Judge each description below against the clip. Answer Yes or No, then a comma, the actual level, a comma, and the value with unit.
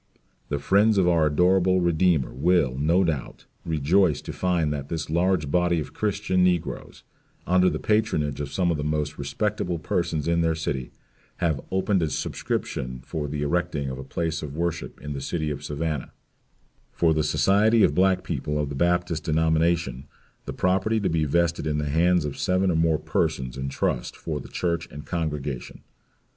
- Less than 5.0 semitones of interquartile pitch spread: Yes, average, 3.4 semitones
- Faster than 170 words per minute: Yes, average, 180 wpm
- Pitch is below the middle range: Yes, very low, 80 Hz